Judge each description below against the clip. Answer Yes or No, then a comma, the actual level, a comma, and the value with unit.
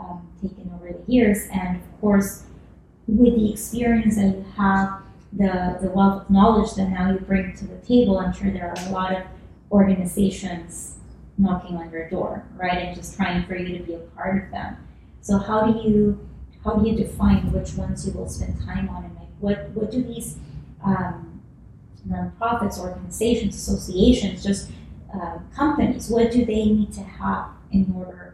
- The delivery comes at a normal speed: Yes, average, 180 wpm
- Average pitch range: Yes, average, 3.0 semitones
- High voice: Yes, high, 195 Hz